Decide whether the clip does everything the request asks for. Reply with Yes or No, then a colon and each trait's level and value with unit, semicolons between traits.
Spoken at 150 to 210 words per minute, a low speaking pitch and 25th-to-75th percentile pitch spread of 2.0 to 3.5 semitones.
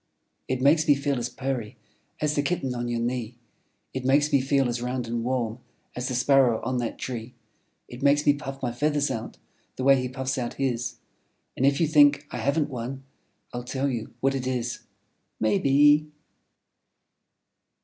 Yes: average, 180 wpm; low, 130 Hz; narrow, 2.5 semitones